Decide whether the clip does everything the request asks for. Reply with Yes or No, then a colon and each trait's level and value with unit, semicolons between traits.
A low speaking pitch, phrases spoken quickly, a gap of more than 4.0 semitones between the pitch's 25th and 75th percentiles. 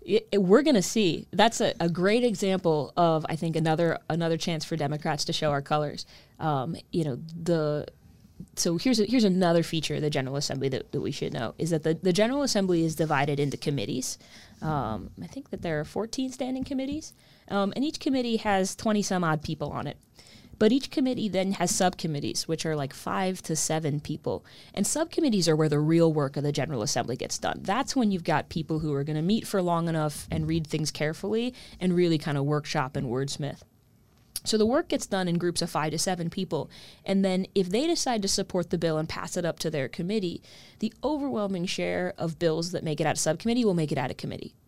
No: medium, 170 Hz; fast, 225 wpm; average, 4.7 semitones